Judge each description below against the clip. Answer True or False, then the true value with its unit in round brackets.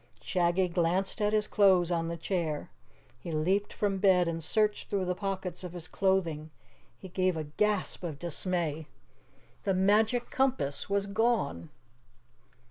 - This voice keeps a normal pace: True (145 wpm)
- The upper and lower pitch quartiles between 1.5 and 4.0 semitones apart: True (3.2 semitones)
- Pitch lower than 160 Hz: False (185 Hz)